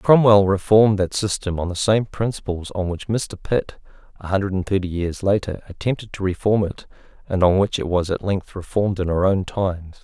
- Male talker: Yes, male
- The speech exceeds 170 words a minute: Yes, fast, 205 wpm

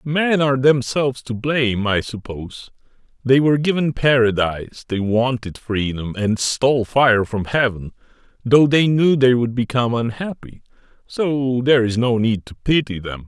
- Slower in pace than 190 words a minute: Yes, average, 155 wpm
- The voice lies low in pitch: Yes, low, 125 Hz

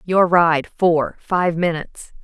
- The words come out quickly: No, slow, 135 wpm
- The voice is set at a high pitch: No, medium, 170 Hz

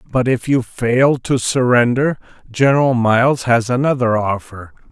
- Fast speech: No, slow, 135 wpm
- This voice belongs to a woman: No, male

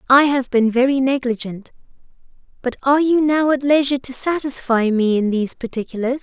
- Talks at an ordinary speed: Yes, average, 155 wpm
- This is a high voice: Yes, very high, 260 Hz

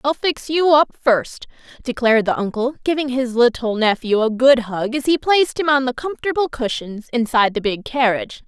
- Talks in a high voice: Yes, very high, 255 Hz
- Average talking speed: Yes, average, 190 wpm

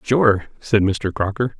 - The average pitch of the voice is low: Yes, low, 105 Hz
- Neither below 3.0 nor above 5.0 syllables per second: Yes, 3.6 syllables/s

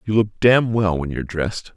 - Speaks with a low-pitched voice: Yes, low, 100 Hz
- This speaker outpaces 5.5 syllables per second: Yes, 5.9 syllables/s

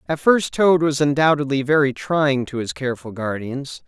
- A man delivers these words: Yes, male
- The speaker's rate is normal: Yes, average, 170 wpm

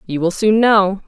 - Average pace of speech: No, fast, 225 wpm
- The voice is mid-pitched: No, high, 200 Hz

